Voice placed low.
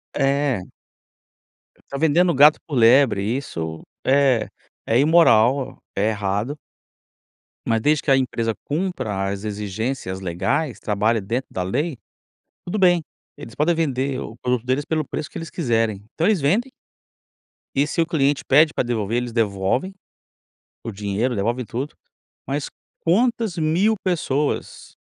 Yes: low, 130 Hz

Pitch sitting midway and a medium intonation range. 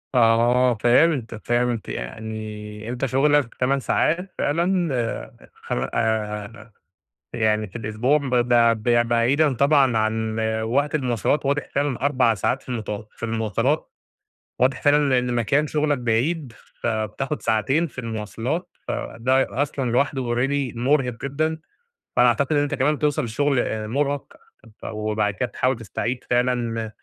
No: low, 125 Hz; average, 4.0 semitones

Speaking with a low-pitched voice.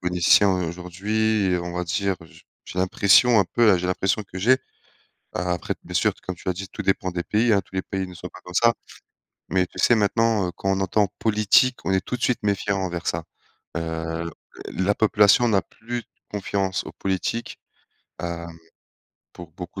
Yes: very low, 95 Hz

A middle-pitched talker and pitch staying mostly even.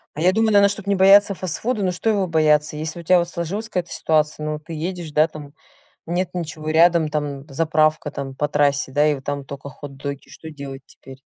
No: medium, 155 Hz; average, 3.7 semitones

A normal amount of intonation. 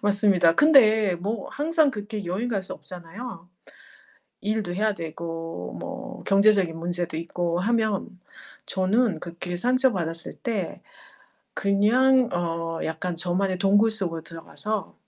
Yes: average, 4.2 semitones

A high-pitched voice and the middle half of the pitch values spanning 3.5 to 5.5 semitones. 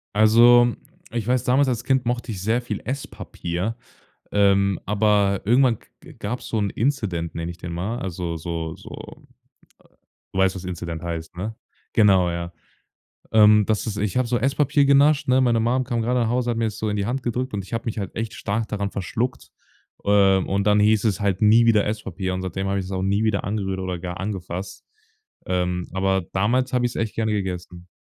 No: low, 105 Hz; average, 3.9 semitones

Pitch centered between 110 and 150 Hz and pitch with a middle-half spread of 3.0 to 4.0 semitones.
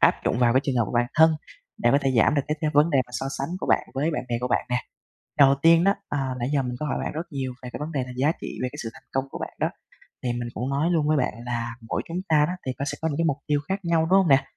Yes: medium, 140 Hz; average, 3.7 semitones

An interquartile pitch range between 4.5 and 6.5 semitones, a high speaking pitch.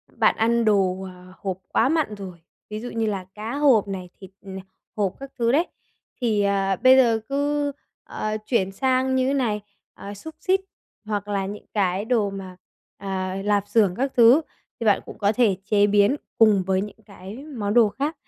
No: average, 4.0 semitones; high, 210 Hz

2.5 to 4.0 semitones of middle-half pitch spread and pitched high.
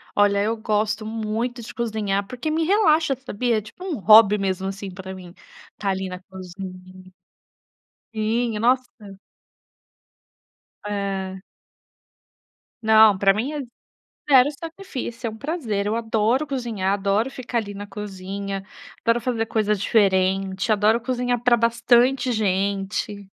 Yes: average, 3.5 semitones; high, 215 Hz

